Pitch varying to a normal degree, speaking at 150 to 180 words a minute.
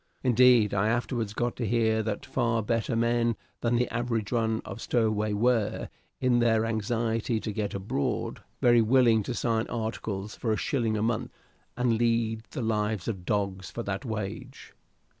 No: narrow, 1.8 semitones; average, 165 wpm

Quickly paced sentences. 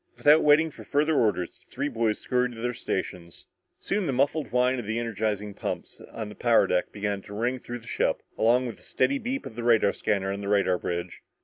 Yes: fast, 225 wpm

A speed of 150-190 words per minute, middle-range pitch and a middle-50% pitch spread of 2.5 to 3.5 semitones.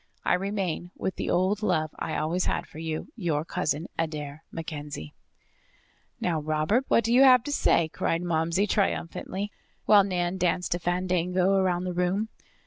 Yes: average, 155 wpm; medium, 180 Hz; average, 3.1 semitones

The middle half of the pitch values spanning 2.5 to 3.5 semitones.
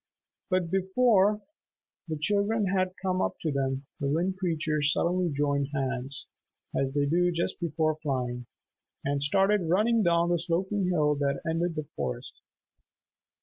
No: average, 4.5 semitones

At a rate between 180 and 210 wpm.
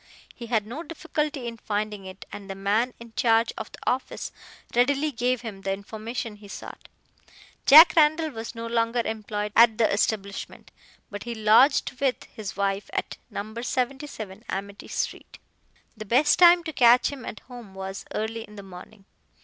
No: average, 170 wpm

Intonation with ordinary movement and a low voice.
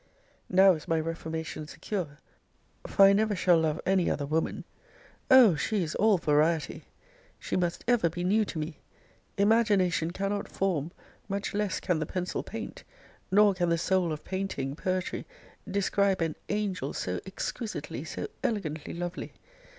No: average, 3.7 semitones; medium, 180 Hz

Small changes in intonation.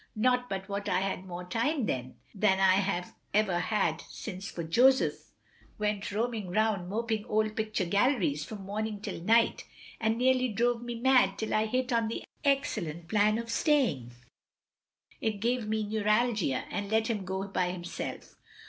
No: average, 3.4 semitones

